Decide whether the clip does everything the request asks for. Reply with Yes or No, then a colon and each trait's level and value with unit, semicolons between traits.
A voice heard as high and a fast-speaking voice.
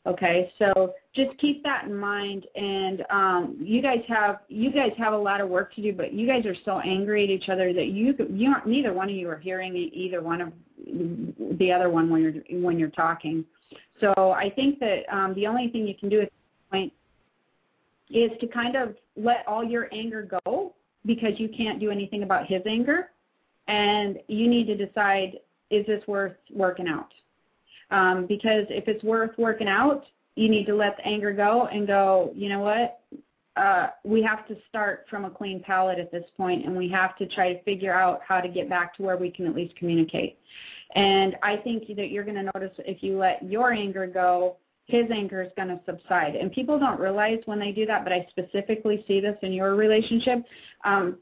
Yes: high, 200 Hz; fast, 210 wpm